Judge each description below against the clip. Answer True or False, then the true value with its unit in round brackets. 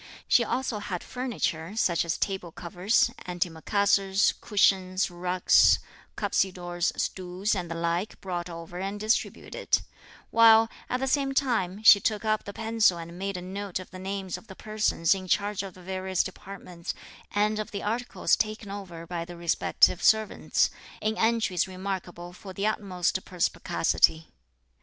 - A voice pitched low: False (190 Hz)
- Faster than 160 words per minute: False (150 wpm)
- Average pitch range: True (3.2 semitones)